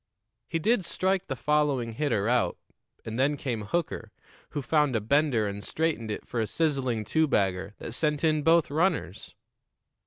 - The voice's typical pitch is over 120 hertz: Yes, medium, 140 Hz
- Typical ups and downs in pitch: No, wide, 5.7 semitones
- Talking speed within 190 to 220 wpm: No, average, 165 wpm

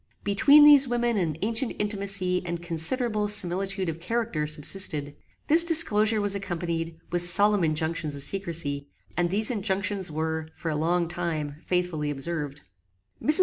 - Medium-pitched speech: Yes, medium, 180 Hz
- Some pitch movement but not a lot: Yes, average, 4.5 semitones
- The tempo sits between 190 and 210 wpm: No, average, 145 wpm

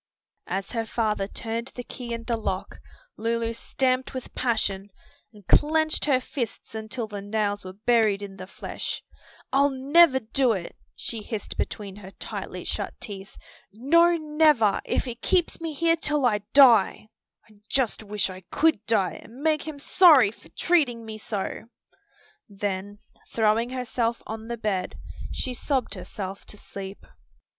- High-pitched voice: Yes, high, 230 Hz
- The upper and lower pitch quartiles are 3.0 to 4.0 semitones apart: No, average, 4.4 semitones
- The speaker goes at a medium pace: Yes, average, 155 wpm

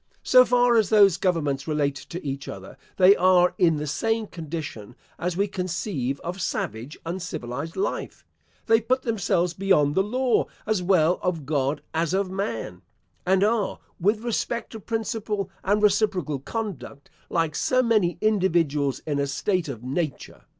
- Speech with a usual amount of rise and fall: No, wide, 5.7 semitones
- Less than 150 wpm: No, average, 155 wpm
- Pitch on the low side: No, medium, 180 Hz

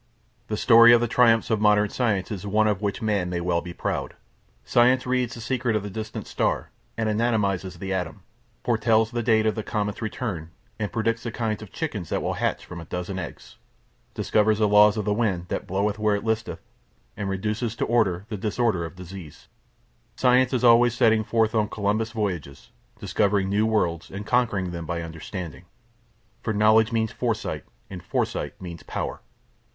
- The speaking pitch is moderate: No, low, 105 Hz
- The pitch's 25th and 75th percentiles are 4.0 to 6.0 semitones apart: No, average, 3.1 semitones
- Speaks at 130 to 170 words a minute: No, average, 185 wpm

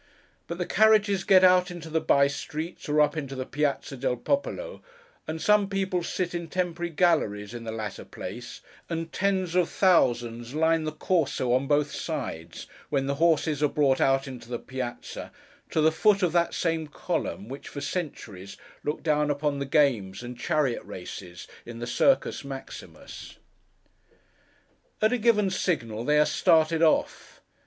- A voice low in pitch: No, medium, 150 Hz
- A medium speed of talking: Yes, average, 165 wpm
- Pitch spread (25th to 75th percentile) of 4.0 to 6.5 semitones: Yes, average, 5.1 semitones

